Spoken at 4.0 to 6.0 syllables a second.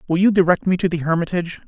No: 7.5 syllables/s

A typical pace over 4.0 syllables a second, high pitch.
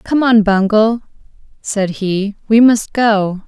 No: 3.4 syllables/s; high, 215 Hz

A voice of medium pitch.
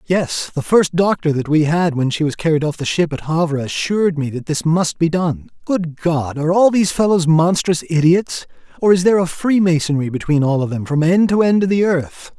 Yes: medium, 165 Hz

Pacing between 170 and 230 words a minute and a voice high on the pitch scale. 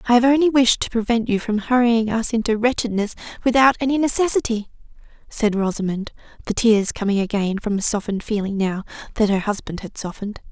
Yes: average, 175 wpm; high, 220 Hz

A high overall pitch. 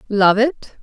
Yes: high, 230 Hz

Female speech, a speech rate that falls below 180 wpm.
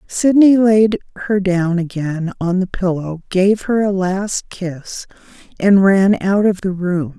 Yes: female; average, 160 wpm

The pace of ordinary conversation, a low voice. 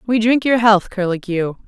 No: average, 180 wpm; high, 210 Hz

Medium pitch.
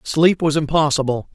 Yes: medium, 150 Hz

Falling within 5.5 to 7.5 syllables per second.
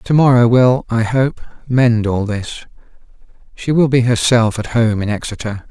No: 4.7 syllables/s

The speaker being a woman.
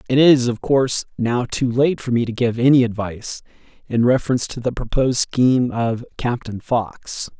No: male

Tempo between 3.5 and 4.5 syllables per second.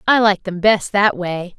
Yes: 4.1 syllables/s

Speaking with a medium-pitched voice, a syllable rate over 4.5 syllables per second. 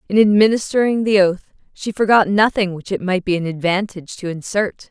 No: high, 195 Hz; 5.5 syllables/s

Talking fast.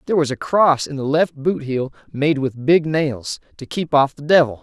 Yes: fast, 235 wpm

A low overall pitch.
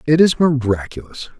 Yes: low, 130 Hz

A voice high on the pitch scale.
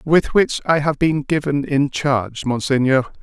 No: medium, 140 Hz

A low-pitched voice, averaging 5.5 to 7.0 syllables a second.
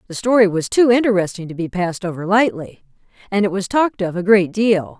No: high, 195 Hz; 6.0 syllables/s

